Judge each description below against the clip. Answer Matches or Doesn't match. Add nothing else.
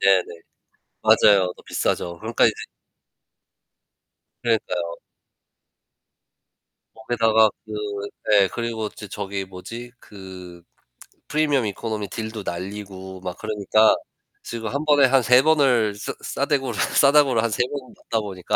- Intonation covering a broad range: Doesn't match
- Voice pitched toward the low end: Matches